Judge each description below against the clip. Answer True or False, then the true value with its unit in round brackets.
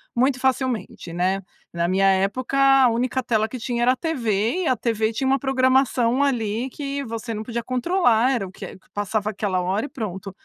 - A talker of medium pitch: False (235 Hz)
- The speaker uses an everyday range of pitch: True (4.0 semitones)